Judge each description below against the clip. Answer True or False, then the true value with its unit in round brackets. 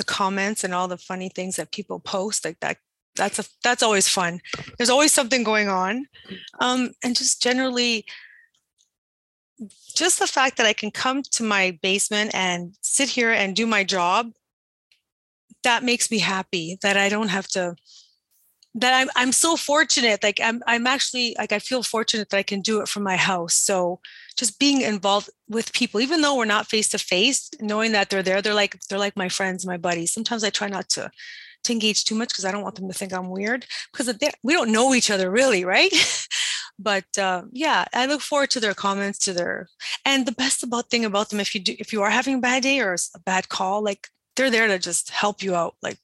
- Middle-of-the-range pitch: False (215 Hz)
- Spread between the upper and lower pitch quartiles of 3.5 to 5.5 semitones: True (4.2 semitones)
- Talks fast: True (210 wpm)